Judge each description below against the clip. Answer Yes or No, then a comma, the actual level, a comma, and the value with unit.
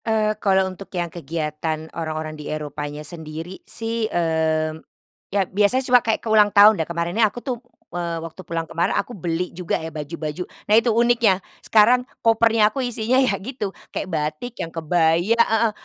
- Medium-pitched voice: Yes, medium, 180 Hz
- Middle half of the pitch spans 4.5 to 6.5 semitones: Yes, wide, 5.6 semitones